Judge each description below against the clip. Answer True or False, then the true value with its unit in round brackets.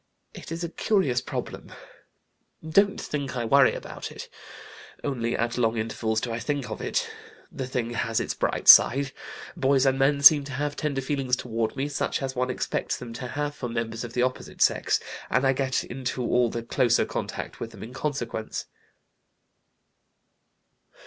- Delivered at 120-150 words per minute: False (175 wpm)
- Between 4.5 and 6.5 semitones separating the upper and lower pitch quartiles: False (3.0 semitones)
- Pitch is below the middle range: True (130 Hz)